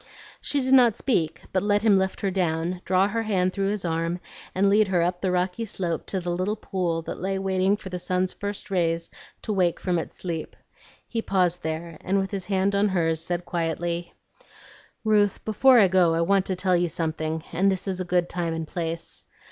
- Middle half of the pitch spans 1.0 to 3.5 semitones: Yes, narrow, 2.5 semitones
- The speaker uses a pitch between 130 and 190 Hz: Yes, medium, 185 Hz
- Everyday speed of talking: No, fast, 210 wpm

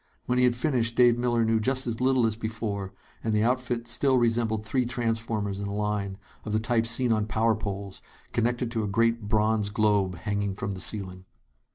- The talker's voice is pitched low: Yes, low, 110 Hz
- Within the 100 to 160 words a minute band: No, average, 200 wpm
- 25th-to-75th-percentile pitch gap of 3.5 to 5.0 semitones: No, narrow, 2.4 semitones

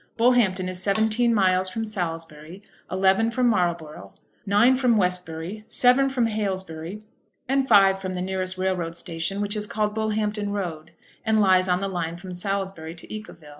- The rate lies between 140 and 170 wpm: Yes, average, 160 wpm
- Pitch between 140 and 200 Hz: Yes, high, 190 Hz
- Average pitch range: Yes, average, 3.2 semitones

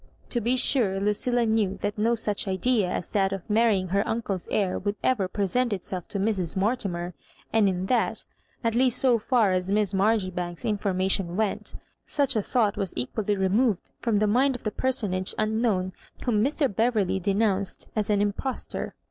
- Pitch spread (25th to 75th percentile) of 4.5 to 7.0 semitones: No, average, 3.2 semitones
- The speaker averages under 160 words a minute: No, average, 185 wpm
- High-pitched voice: Yes, high, 210 Hz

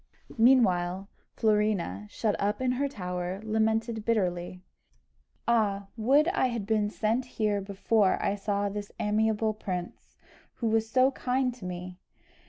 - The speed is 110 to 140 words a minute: Yes, slow, 135 wpm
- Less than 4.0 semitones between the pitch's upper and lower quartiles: Yes, average, 2.8 semitones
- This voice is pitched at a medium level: No, high, 215 Hz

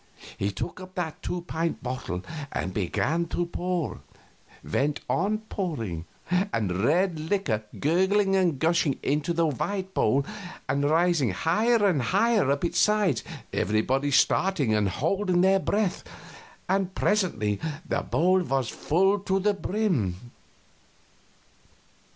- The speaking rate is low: Yes, slow, 125 wpm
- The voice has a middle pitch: Yes, medium, 170 Hz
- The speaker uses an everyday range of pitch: No, wide, 6.4 semitones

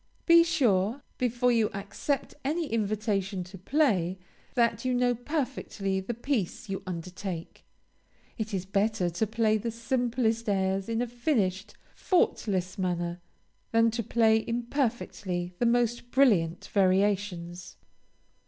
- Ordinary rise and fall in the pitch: Yes, average, 4.2 semitones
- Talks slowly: Yes, slow, 125 wpm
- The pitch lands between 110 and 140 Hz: No, high, 220 Hz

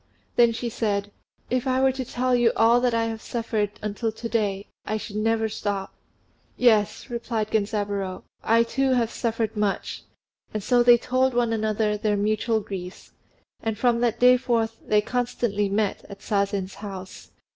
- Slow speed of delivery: No, average, 165 wpm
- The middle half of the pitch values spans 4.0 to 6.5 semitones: No, narrow, 2.5 semitones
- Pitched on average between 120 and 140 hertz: No, high, 225 Hz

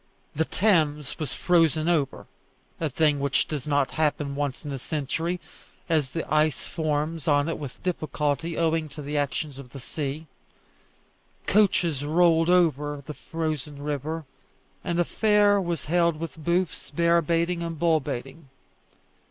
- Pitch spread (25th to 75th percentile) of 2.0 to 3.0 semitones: Yes, narrow, 2.6 semitones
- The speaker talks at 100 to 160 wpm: Yes, average, 150 wpm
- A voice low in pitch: No, medium, 155 Hz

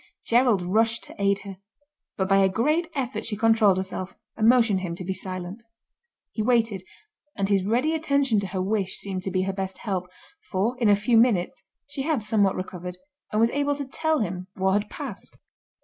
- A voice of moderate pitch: No, high, 205 Hz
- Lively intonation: No, average, 3.8 semitones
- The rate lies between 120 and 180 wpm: No, average, 195 wpm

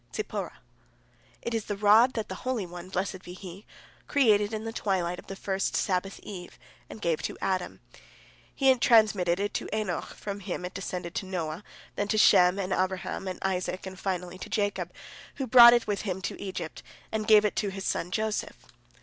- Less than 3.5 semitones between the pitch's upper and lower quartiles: Yes, average, 2.8 semitones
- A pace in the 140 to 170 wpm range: No, average, 190 wpm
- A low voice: No, high, 195 Hz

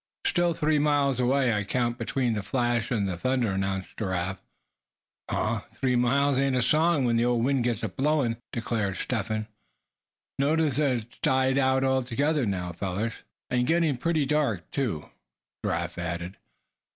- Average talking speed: Yes, average, 160 wpm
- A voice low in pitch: Yes, low, 125 Hz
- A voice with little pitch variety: No, average, 4.3 semitones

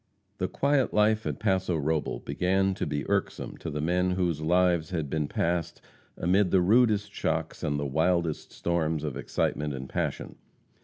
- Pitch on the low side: Yes, very low, 85 Hz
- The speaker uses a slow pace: No, average, 165 wpm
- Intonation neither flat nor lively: Yes, average, 3.6 semitones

